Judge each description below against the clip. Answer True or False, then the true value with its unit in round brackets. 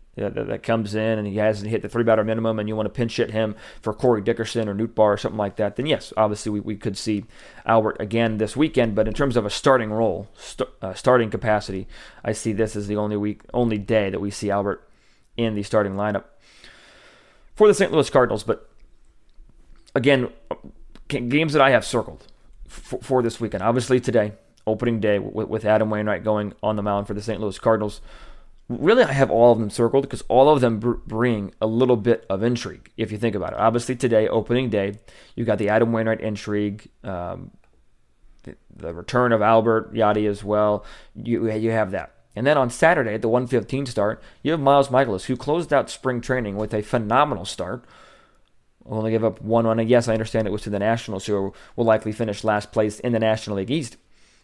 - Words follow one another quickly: True (215 wpm)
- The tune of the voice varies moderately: False (2.1 semitones)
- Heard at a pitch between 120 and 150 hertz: False (110 Hz)